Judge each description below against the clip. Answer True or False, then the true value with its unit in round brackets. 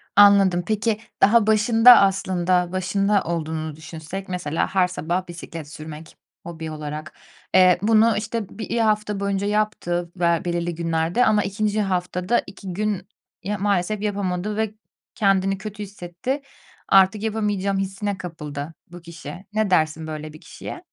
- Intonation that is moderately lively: True (3.4 semitones)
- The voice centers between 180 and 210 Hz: True (190 Hz)